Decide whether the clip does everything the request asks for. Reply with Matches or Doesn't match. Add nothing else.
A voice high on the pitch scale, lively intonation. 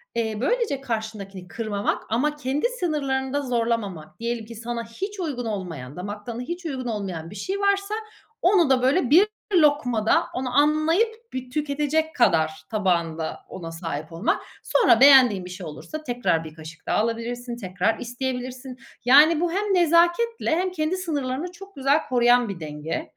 Matches